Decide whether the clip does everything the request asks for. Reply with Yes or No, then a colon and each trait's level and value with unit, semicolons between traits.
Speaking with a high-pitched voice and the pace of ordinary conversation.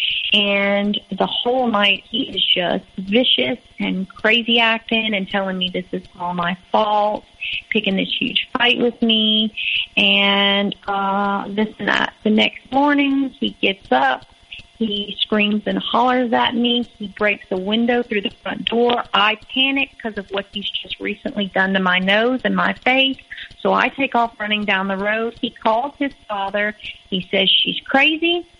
Yes: high, 215 Hz; average, 170 wpm